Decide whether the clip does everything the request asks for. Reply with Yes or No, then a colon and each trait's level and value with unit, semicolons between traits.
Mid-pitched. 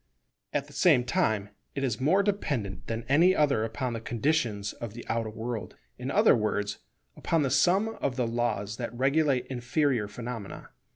No: low, 125 Hz